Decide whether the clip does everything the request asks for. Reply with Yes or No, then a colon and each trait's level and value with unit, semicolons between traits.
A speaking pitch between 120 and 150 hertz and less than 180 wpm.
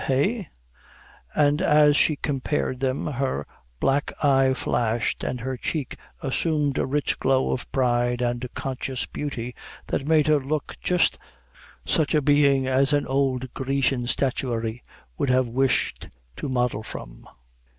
Yes: low, 135 Hz; average, 140 wpm